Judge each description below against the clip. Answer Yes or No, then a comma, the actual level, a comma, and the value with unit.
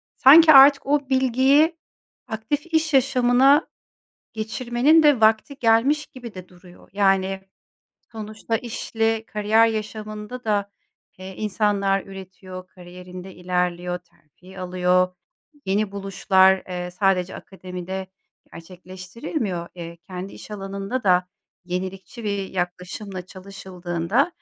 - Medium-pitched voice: No, high, 195 Hz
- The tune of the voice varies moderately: Yes, average, 3.8 semitones